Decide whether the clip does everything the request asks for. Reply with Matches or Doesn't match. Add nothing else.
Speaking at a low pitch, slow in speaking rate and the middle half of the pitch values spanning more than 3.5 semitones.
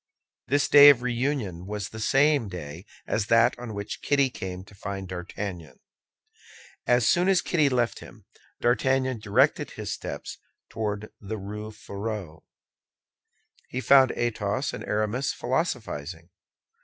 Matches